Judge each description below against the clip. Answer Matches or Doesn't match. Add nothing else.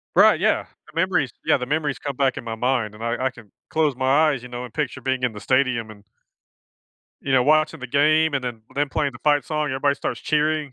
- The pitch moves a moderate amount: Matches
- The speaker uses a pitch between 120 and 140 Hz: Matches